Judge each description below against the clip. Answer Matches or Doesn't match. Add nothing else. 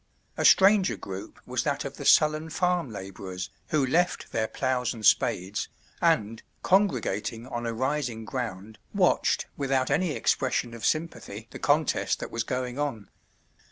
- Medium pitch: Doesn't match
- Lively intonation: Matches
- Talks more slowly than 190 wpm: Matches